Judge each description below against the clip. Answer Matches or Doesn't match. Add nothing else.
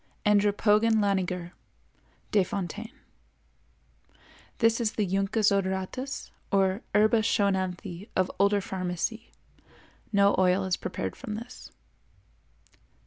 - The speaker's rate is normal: Doesn't match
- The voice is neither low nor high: Doesn't match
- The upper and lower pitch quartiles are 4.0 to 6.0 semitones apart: Doesn't match